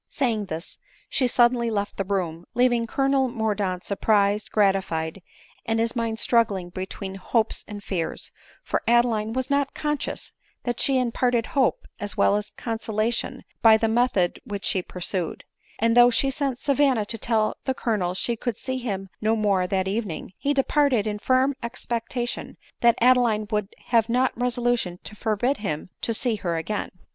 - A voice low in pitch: No, high, 225 Hz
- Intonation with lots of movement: No, average, 3.5 semitones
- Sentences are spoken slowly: No, average, 165 wpm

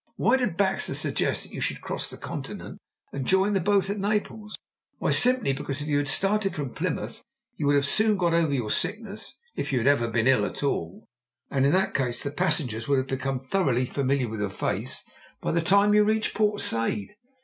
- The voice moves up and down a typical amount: No, wide, 7.3 semitones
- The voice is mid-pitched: Yes, medium, 145 Hz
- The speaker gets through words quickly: Yes, fast, 215 wpm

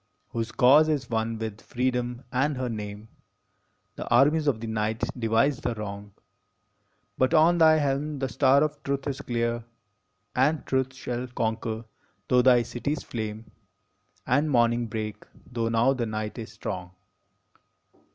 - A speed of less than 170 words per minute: Yes, average, 145 wpm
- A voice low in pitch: Yes, low, 120 Hz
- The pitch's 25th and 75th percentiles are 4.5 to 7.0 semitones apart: No, average, 3.5 semitones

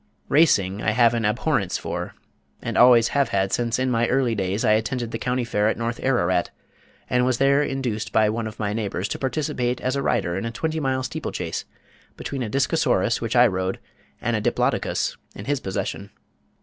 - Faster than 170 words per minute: Yes, average, 195 wpm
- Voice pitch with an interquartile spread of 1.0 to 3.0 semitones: No, average, 3.7 semitones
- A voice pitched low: Yes, low, 115 Hz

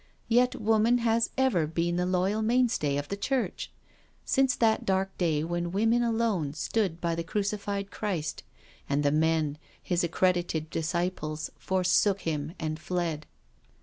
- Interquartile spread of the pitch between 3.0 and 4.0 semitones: No, average, 5.1 semitones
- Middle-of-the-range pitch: Yes, medium, 180 Hz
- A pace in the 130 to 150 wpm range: Yes, average, 145 wpm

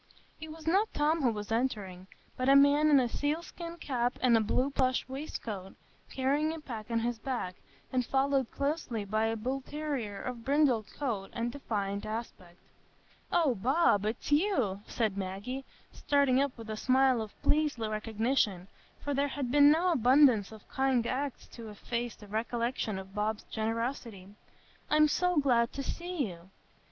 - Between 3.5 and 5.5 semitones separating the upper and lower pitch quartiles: Yes, average, 4.6 semitones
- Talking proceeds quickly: No, average, 165 wpm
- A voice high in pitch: Yes, very high, 250 Hz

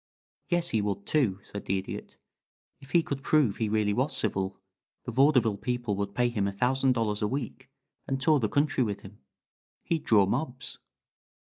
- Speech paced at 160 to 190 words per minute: Yes, average, 180 wpm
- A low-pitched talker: Yes, low, 120 Hz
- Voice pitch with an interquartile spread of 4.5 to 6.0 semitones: Yes, average, 4.9 semitones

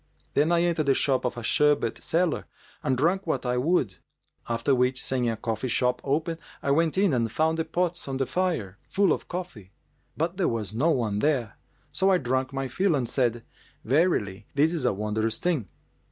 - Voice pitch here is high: No, low, 135 Hz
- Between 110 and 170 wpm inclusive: No, average, 195 wpm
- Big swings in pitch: Yes, wide, 5.8 semitones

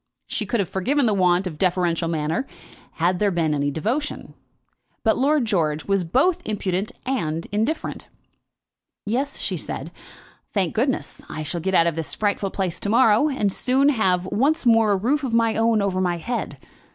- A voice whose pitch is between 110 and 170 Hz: No, high, 200 Hz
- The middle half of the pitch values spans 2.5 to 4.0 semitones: No, wide, 5.6 semitones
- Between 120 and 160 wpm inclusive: No, average, 175 wpm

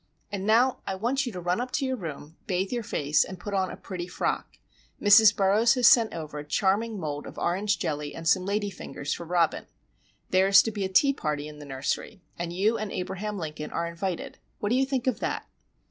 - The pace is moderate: No, fast, 225 wpm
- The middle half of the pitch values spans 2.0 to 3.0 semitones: No, average, 4.3 semitones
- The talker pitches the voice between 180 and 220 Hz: Yes, high, 190 Hz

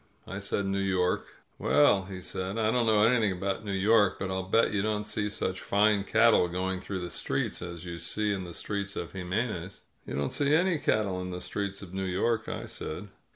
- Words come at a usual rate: No, fast, 220 wpm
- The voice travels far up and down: No, narrow, 2.5 semitones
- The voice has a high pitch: No, low, 100 Hz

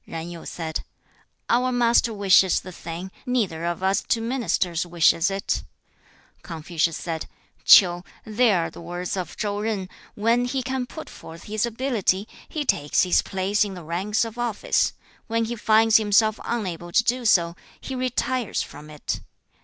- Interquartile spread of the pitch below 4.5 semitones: No, average, 5.1 semitones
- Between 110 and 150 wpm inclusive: No, average, 170 wpm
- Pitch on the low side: No, high, 205 Hz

